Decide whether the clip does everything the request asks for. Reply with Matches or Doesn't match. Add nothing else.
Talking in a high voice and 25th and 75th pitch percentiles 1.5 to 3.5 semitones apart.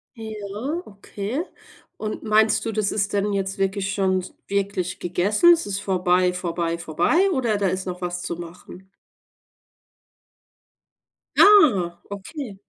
Matches